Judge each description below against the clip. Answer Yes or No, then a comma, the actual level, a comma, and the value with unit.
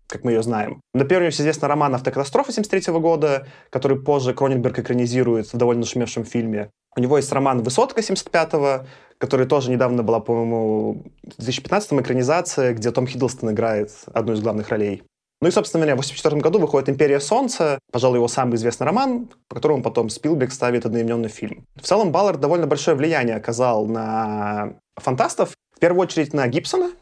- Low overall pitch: Yes, low, 130 Hz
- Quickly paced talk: Yes, fast, 175 wpm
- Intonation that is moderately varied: Yes, average, 4.4 semitones